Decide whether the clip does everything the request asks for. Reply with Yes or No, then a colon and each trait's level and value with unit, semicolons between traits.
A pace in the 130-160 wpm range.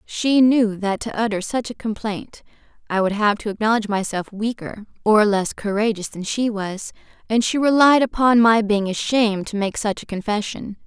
No: average, 180 wpm